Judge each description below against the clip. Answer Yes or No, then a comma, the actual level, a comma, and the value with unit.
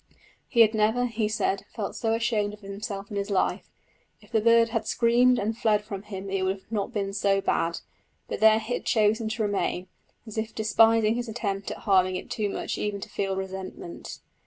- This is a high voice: Yes, high, 215 Hz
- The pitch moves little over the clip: Yes, narrow, 2.3 semitones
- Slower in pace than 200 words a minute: No, fast, 205 wpm